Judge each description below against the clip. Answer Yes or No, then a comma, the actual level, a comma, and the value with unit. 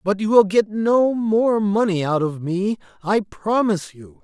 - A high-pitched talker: Yes, high, 200 Hz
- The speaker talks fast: No, average, 185 wpm